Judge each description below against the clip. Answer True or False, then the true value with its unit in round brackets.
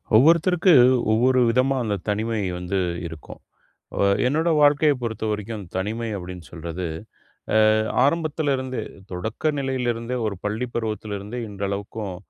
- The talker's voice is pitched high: False (115 Hz)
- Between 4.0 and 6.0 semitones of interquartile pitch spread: True (4.7 semitones)